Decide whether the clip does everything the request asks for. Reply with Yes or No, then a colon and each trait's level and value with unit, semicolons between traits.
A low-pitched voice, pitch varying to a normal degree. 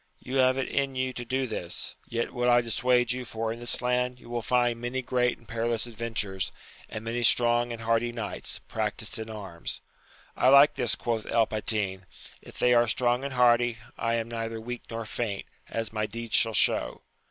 No: low, 120 Hz; narrow, 1.6 semitones